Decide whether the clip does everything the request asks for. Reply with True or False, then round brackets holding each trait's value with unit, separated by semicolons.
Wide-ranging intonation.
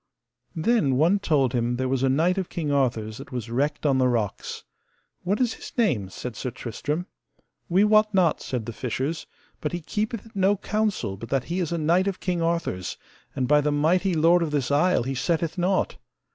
True (6.0 semitones)